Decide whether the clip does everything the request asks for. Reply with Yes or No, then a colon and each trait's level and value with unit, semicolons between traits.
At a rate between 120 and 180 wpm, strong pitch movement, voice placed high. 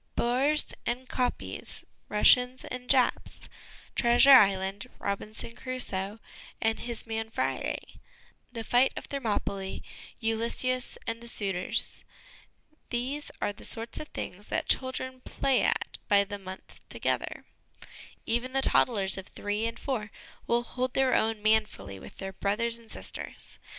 No: slow, 135 wpm; average, 3.6 semitones; high, 230 Hz